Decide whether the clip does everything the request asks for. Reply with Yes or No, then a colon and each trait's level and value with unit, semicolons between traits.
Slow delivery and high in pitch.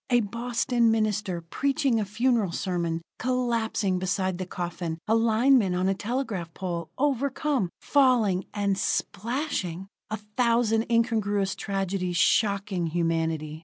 Yes: slow, 120 wpm; high, 205 Hz